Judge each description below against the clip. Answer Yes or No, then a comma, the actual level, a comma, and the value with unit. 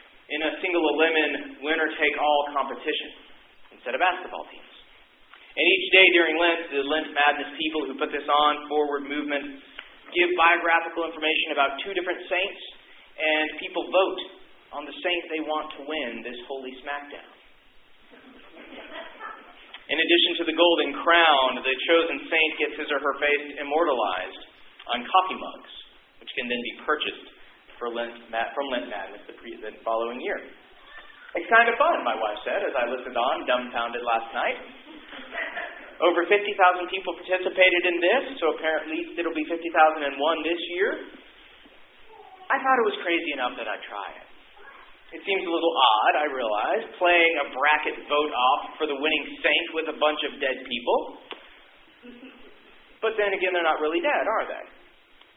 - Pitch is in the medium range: Yes, medium, 160 Hz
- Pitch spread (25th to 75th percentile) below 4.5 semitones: Yes, average, 3.5 semitones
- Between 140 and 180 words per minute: Yes, average, 165 wpm